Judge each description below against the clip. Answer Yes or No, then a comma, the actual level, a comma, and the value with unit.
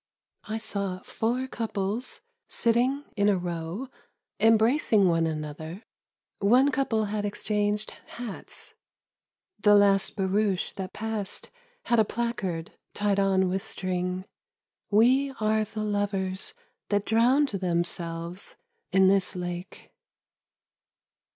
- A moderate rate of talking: No, slow, 115 wpm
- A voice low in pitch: No, high, 205 Hz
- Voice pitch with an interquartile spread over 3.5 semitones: No, average, 3.1 semitones